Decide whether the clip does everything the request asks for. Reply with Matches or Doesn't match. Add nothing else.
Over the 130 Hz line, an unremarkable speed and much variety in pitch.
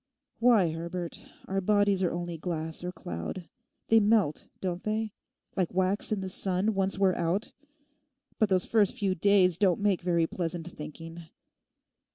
Doesn't match